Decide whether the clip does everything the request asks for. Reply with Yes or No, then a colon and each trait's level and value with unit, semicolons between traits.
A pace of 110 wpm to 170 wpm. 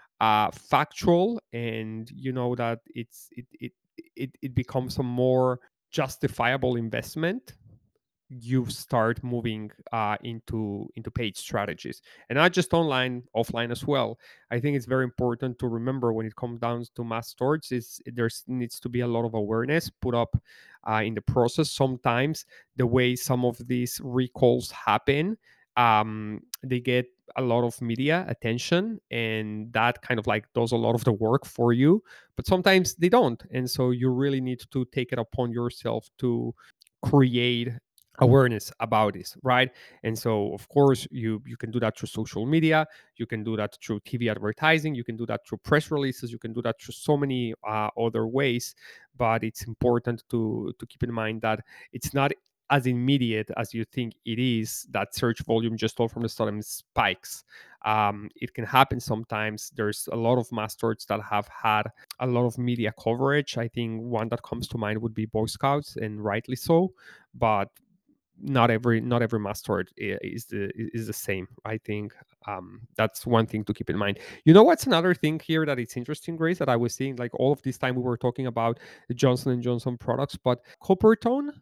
No: average, 190 wpm